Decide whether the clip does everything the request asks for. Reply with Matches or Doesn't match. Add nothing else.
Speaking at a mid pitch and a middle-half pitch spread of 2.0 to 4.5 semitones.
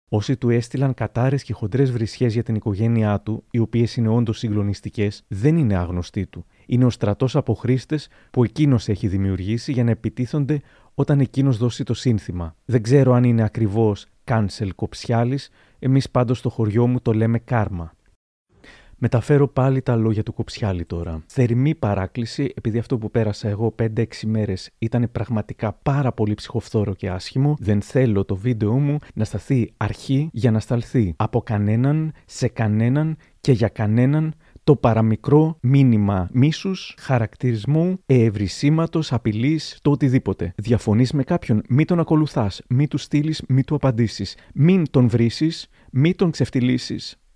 Doesn't match